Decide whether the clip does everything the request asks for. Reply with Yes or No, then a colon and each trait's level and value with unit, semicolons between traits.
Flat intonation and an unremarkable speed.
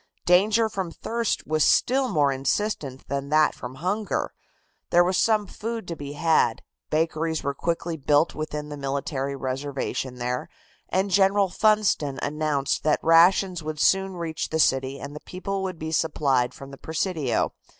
No: average, 5.2 semitones; average, 160 wpm